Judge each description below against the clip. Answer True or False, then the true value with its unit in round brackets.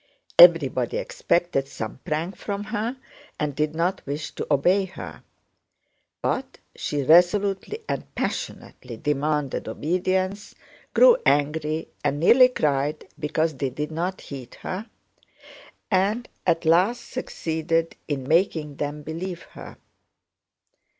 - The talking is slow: True (115 wpm)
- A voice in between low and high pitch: True (165 Hz)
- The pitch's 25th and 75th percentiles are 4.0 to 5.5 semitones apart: True (4.4 semitones)